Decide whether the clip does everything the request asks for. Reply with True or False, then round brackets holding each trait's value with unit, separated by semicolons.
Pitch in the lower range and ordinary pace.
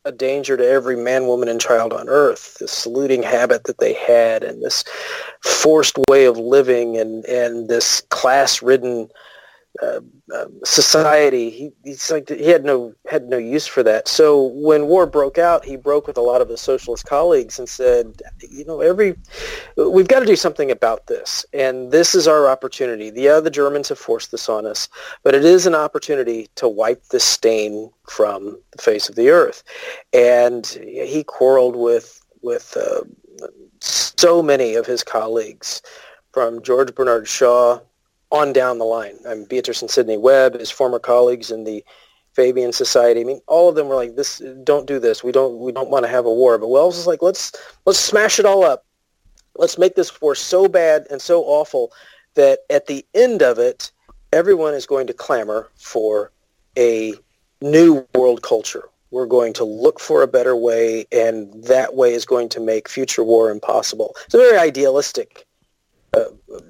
False (145 Hz; 185 wpm)